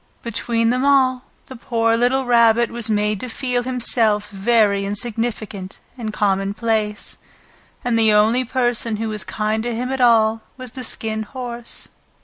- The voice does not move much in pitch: Yes, narrow, 2.3 semitones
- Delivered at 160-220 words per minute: No, average, 150 wpm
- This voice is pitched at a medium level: No, high, 230 Hz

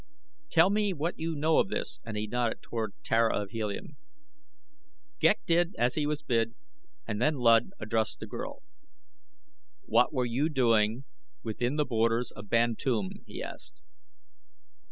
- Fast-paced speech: No, average, 150 wpm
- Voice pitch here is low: Yes, low, 120 Hz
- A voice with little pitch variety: No, average, 5.3 semitones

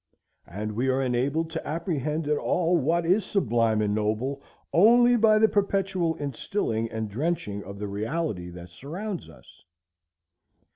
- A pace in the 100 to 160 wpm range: Yes, average, 145 wpm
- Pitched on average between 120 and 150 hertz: Yes, medium, 140 Hz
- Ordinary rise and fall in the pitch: No, wide, 8.2 semitones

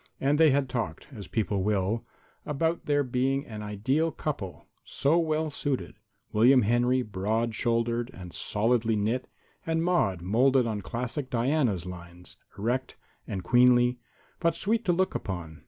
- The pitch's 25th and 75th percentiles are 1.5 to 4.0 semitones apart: No, average, 5.1 semitones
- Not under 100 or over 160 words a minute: Yes, average, 145 wpm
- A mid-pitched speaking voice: No, low, 120 Hz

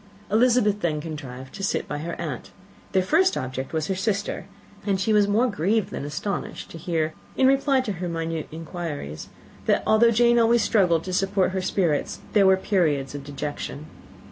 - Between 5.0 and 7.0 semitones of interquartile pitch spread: Yes, average, 5.3 semitones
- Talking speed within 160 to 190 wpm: Yes, average, 180 wpm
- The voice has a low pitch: No, medium, 185 Hz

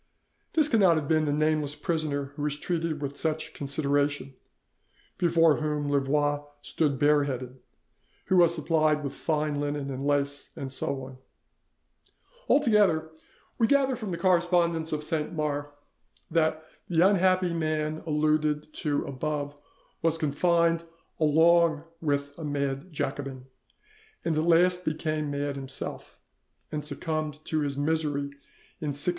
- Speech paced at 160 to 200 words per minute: No, slow, 135 wpm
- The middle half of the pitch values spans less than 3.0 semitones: Yes, narrow, 2.4 semitones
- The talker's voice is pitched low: No, medium, 155 Hz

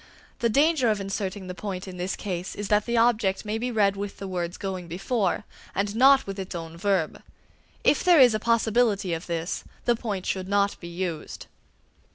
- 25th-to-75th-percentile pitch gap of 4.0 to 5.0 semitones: No, average, 3.4 semitones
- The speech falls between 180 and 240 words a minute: Yes, average, 200 wpm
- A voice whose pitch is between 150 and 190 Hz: No, high, 200 Hz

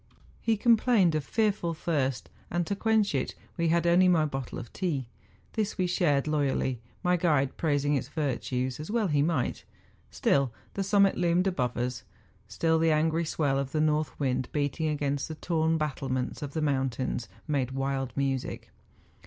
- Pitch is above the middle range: No, medium, 150 Hz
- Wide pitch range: No, average, 4.2 semitones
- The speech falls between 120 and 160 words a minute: No, average, 170 wpm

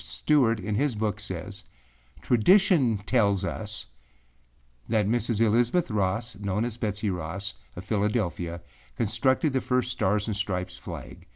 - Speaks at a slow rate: Yes, slow, 130 wpm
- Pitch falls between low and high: No, low, 105 Hz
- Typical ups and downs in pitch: Yes, average, 3.2 semitones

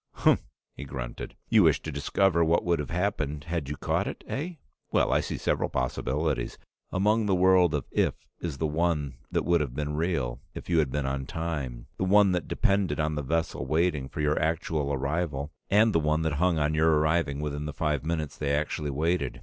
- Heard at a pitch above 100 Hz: No, very low, 75 Hz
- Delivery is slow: No, fast, 205 wpm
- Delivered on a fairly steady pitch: No, average, 3.0 semitones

